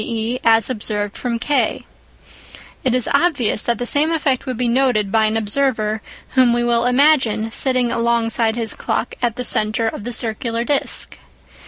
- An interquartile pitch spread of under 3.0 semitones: Yes, narrow, 2.5 semitones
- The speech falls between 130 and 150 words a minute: No, average, 170 wpm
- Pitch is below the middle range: No, high, 235 Hz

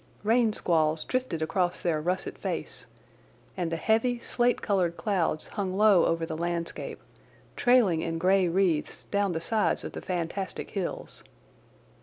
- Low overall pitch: No, medium, 180 Hz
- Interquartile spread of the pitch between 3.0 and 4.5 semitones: Yes, average, 3.9 semitones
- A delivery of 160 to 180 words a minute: No, average, 145 wpm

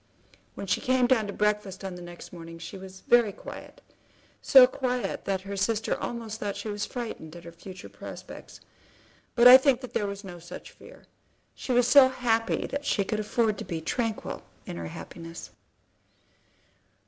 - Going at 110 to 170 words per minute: No, average, 180 wpm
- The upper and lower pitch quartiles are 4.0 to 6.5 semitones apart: Yes, average, 4.4 semitones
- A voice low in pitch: No, high, 210 Hz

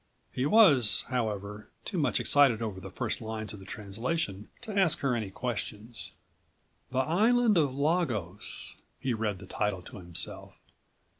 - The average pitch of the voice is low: Yes, low, 115 Hz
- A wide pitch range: Yes, wide, 6.1 semitones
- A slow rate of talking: No, average, 150 wpm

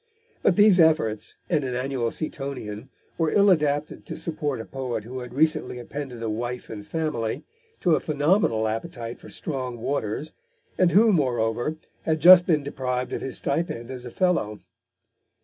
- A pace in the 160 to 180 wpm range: Yes, average, 165 wpm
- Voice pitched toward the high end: No, low, 135 Hz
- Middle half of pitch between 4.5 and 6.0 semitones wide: Yes, average, 5.0 semitones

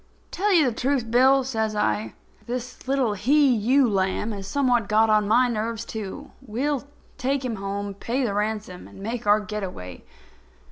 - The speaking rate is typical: Yes, average, 175 wpm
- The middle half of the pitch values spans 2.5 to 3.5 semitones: No, average, 3.9 semitones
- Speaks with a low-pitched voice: No, high, 225 Hz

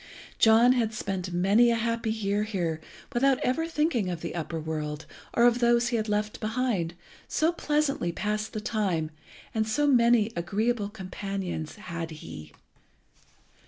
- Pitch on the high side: Yes, high, 215 Hz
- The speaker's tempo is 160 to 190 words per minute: No, average, 145 wpm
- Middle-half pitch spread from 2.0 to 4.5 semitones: No, average, 5.1 semitones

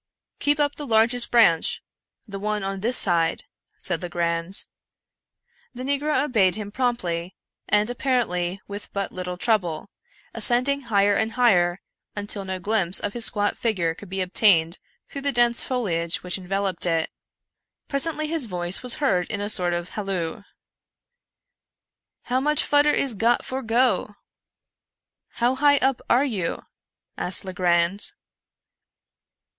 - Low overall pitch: No, high, 205 Hz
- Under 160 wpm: Yes, average, 150 wpm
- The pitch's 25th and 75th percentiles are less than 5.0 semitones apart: No, wide, 5.5 semitones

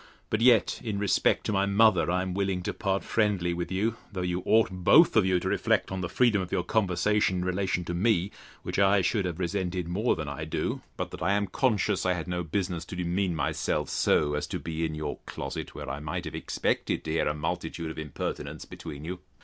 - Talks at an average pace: No, fast, 230 wpm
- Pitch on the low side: Yes, very low, 90 Hz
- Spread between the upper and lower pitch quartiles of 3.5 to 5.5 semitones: No, average, 2.8 semitones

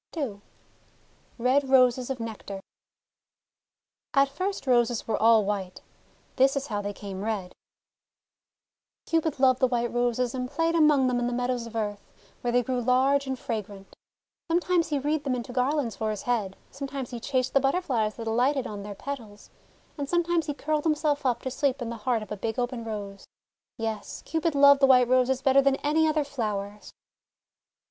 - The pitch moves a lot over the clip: No, average, 3.9 semitones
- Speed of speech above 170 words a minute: Yes, average, 185 wpm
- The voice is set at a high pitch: Yes, very high, 250 Hz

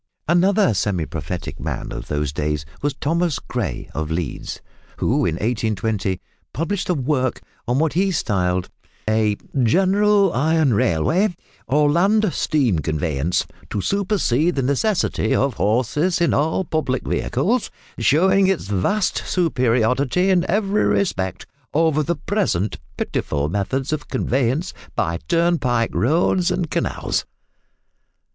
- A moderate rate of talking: No, slow, 125 wpm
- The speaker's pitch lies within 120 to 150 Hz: Yes, medium, 140 Hz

